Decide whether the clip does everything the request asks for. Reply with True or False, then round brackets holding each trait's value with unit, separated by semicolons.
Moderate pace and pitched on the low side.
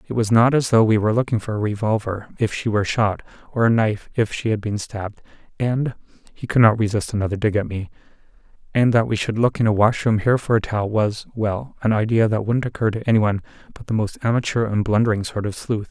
False (225 wpm; 110 Hz)